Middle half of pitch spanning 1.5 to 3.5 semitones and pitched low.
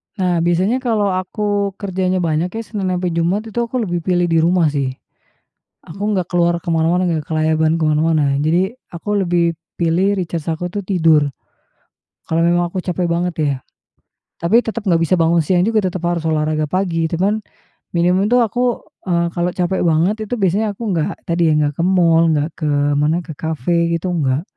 No: average, 2.7 semitones; medium, 175 Hz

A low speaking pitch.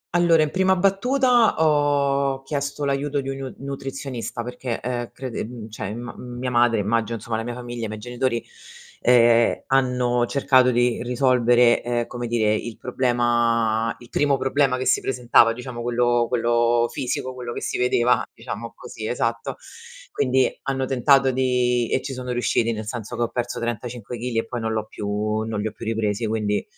Yes: low, 120 Hz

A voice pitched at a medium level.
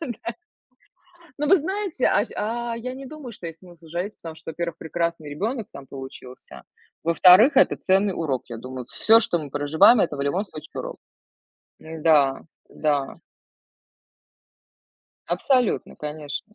Yes: medium, 170 Hz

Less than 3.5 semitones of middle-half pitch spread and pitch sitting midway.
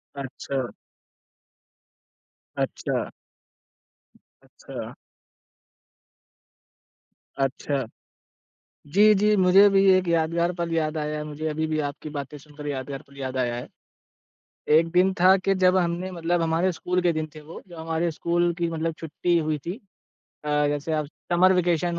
Yes: average, 2.8 semitones; medium, 165 Hz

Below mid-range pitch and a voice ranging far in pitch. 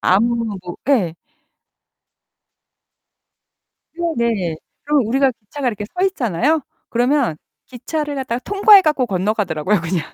No: high, 235 Hz; wide, 6.9 semitones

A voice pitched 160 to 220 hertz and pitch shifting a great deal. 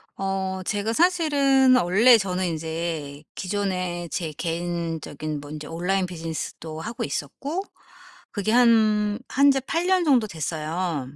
Yes: medium, 185 Hz; wide, 6.1 semitones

